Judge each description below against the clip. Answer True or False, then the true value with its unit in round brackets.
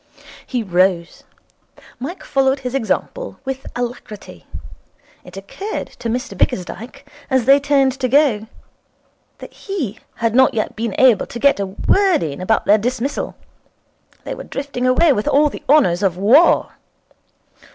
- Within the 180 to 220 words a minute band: False (145 wpm)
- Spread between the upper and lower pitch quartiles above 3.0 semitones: True (5.0 semitones)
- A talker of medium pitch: False (250 Hz)